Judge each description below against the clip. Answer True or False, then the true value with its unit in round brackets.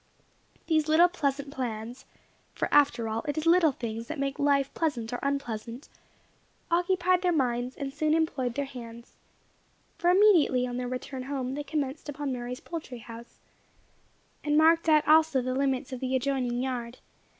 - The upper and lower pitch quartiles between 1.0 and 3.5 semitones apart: False (3.9 semitones)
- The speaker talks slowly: False (160 wpm)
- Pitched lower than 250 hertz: False (275 Hz)